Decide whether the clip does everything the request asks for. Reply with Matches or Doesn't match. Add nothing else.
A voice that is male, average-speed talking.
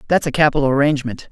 Matches